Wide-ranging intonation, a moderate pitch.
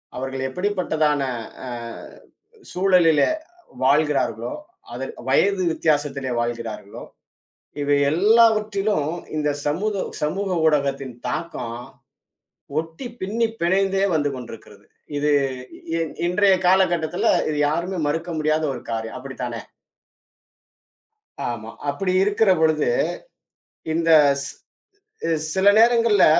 Yes: wide, 5.9 semitones; medium, 160 Hz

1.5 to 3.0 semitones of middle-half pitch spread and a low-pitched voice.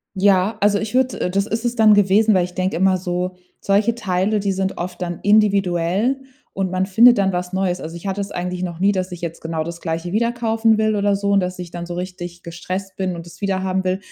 No: narrow, 2.4 semitones; high, 190 Hz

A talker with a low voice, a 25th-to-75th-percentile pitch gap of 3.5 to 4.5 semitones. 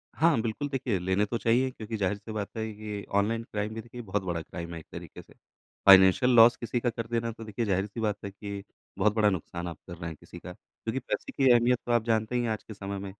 No: low, 110 Hz; average, 2.9 semitones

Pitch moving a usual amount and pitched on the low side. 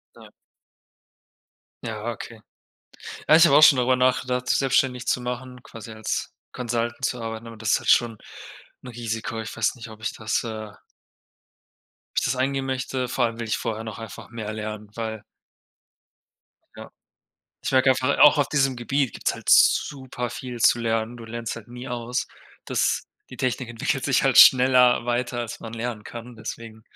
No: narrow, 2.2 semitones; low, 120 Hz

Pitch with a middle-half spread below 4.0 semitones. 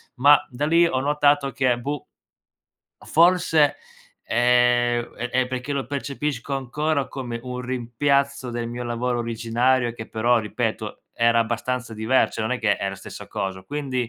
Yes: average, 2.9 semitones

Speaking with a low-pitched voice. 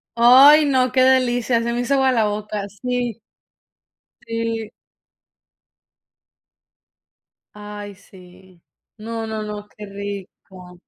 No: high, 225 Hz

